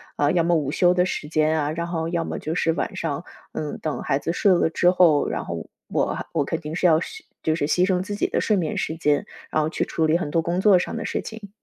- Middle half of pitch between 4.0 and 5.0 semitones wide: No, narrow, 2.4 semitones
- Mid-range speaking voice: Yes, medium, 165 Hz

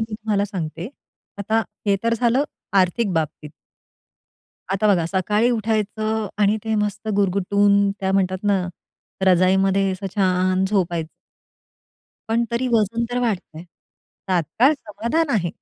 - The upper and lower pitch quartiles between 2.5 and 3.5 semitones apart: Yes, average, 3.0 semitones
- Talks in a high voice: Yes, high, 200 Hz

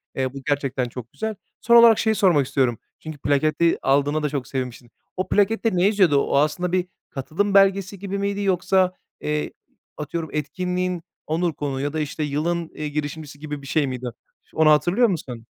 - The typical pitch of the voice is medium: Yes, medium, 155 Hz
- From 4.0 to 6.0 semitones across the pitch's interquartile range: Yes, average, 4.6 semitones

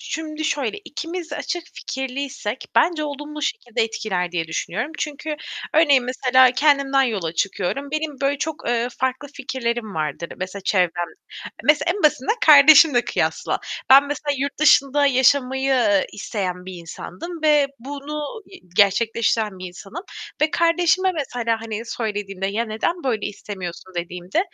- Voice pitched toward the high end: Yes, very high, 260 Hz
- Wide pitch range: Yes, wide, 6.3 semitones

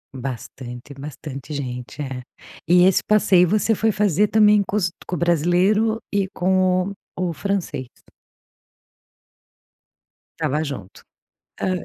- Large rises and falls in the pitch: Yes, wide, 6.1 semitones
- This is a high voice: No, medium, 180 Hz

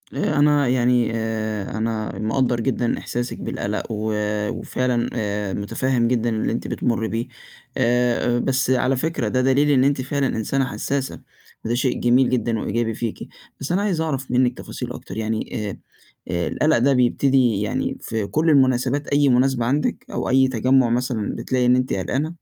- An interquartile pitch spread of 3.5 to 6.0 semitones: No, average, 2.9 semitones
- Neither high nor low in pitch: No, low, 125 Hz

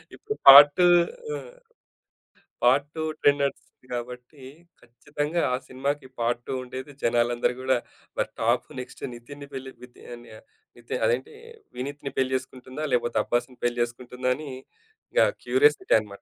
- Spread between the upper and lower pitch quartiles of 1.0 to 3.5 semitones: Yes, average, 2.9 semitones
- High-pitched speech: No, low, 130 Hz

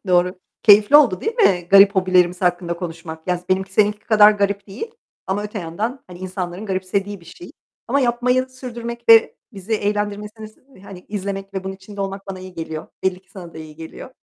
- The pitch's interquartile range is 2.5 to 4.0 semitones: Yes, average, 2.8 semitones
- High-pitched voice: Yes, high, 195 Hz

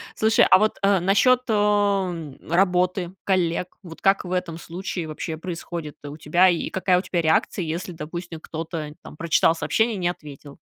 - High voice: No, medium, 175 Hz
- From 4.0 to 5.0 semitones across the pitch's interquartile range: No, average, 2.9 semitones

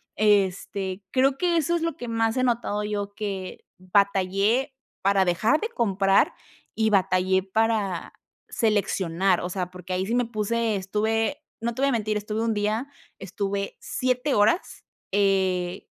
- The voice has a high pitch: Yes, high, 205 Hz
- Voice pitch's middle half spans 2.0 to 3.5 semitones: Yes, average, 3.2 semitones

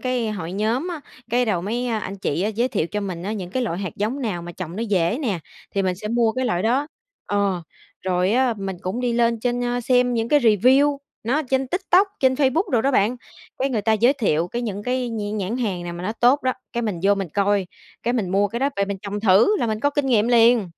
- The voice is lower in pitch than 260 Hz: Yes, high, 225 Hz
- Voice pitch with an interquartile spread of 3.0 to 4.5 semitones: Yes, average, 4.1 semitones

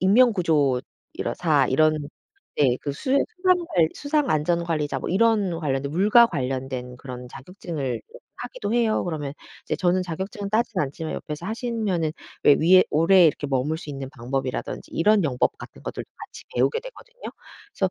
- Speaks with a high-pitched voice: No, medium, 165 Hz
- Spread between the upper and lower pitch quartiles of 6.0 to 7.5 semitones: Yes, wide, 7.0 semitones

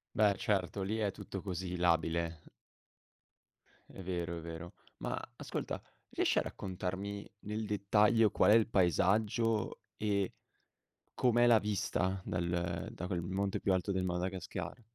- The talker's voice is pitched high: No, very low, 95 Hz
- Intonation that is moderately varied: Yes, average, 3.0 semitones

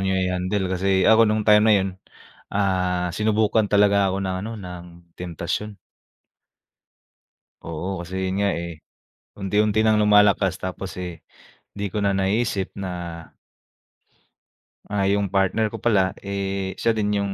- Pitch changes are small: Yes, narrow, 1.9 semitones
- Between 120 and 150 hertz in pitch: No, low, 100 Hz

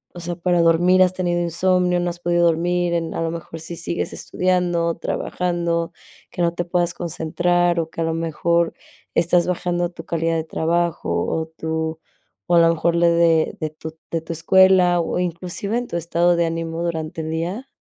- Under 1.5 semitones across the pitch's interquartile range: Yes, narrow, 1.1 semitones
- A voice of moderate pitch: Yes, medium, 170 Hz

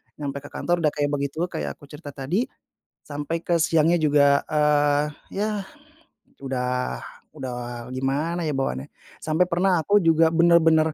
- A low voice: No, medium, 150 Hz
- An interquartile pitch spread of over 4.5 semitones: No, average, 3.0 semitones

